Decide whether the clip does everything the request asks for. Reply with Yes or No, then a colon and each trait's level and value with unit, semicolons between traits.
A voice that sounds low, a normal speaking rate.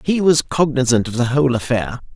Yes: low, 130 Hz; average, 195 wpm